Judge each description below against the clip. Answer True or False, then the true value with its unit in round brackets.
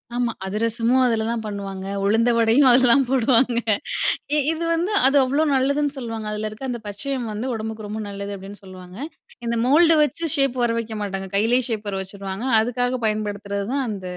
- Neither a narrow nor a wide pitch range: True (4.0 semitones)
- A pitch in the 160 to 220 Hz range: False (230 Hz)